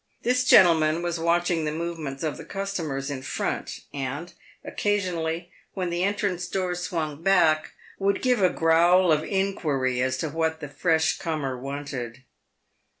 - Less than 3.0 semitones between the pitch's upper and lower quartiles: No, average, 3.6 semitones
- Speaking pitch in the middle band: Yes, medium, 165 Hz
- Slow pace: No, average, 150 wpm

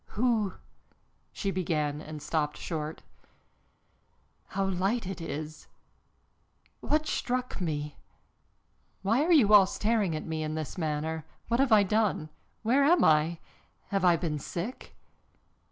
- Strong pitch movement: Yes, wide, 6.0 semitones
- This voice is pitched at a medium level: Yes, medium, 180 Hz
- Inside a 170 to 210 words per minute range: No, slow, 135 wpm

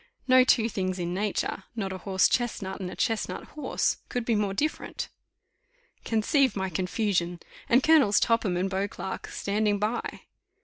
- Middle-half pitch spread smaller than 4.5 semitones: Yes, average, 3.6 semitones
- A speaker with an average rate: Yes, average, 150 wpm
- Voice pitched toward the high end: Yes, high, 205 Hz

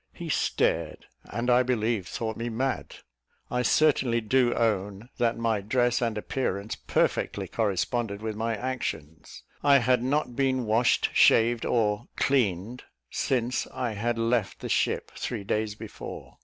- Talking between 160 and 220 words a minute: No, average, 140 wpm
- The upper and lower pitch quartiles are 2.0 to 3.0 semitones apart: Yes, average, 2.7 semitones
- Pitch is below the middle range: Yes, low, 115 Hz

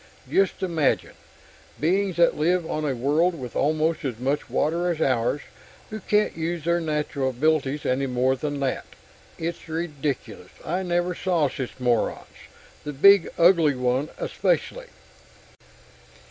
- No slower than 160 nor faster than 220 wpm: No, slow, 135 wpm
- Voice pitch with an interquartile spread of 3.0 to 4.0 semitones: No, average, 4.4 semitones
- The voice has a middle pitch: Yes, medium, 155 Hz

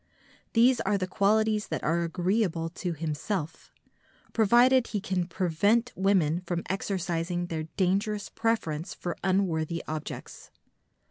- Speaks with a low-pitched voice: No, medium, 185 Hz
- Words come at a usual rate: No, slow, 120 wpm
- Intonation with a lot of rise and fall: No, average, 3.9 semitones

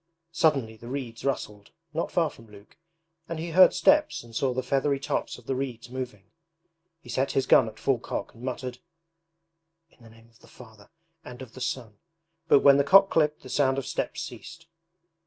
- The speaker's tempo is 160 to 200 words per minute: Yes, average, 195 wpm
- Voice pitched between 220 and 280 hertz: No, low, 130 Hz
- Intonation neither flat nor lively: Yes, average, 3.5 semitones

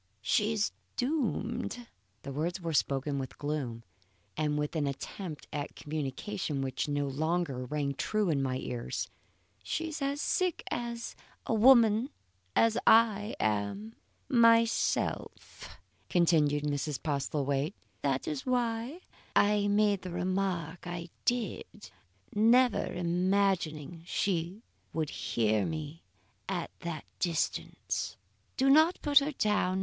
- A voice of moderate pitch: Yes, medium, 175 Hz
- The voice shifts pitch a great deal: Yes, wide, 7.3 semitones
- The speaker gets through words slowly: Yes, slow, 115 wpm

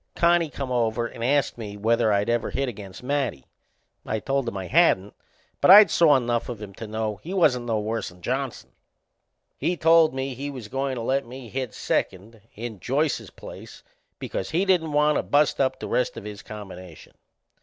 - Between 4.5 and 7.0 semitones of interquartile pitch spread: Yes, average, 4.8 semitones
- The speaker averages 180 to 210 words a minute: Yes, average, 190 wpm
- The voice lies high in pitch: No, low, 125 Hz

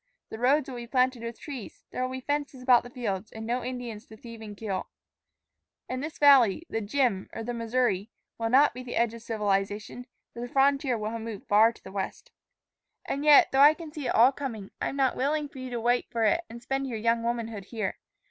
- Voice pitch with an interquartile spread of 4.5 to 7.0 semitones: No, average, 3.1 semitones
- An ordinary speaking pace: No, fast, 235 wpm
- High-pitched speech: Yes, high, 240 Hz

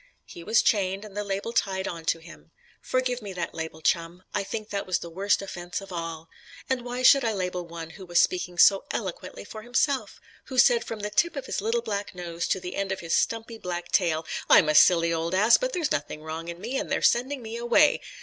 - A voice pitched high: Yes, high, 195 Hz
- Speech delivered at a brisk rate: Yes, fast, 235 wpm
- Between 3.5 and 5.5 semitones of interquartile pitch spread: Yes, average, 5.1 semitones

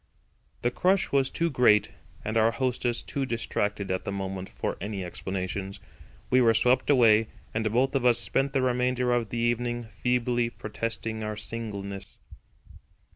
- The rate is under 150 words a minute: No, average, 155 wpm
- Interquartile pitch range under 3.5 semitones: Yes, average, 3.1 semitones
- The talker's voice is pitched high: No, low, 115 Hz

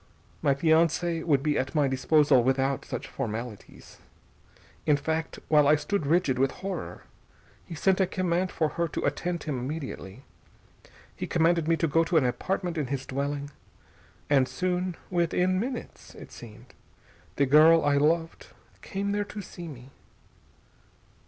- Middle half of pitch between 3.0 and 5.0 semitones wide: Yes, average, 3.9 semitones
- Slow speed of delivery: No, average, 150 wpm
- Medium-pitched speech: Yes, medium, 155 Hz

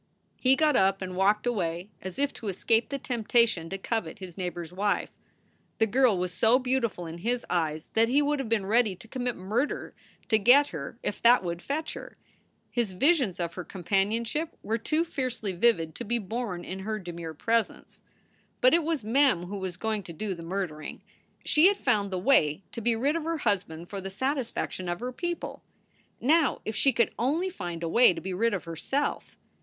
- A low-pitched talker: No, high, 215 Hz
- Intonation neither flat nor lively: No, wide, 5.7 semitones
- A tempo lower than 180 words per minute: No, fast, 205 wpm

